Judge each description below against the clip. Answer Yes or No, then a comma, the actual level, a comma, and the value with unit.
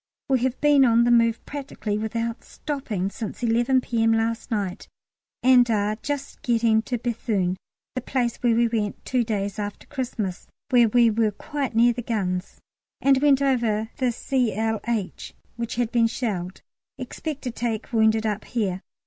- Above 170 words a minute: No, average, 165 wpm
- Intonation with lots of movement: No, narrow, 2.4 semitones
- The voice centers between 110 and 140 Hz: No, high, 230 Hz